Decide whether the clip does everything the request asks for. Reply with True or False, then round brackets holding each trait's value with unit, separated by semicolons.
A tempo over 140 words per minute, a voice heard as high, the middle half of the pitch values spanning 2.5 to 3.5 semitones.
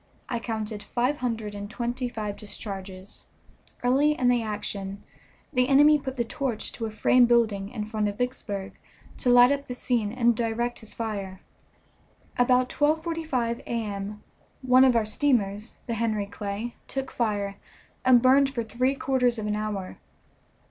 True (155 wpm; 235 Hz; 3.2 semitones)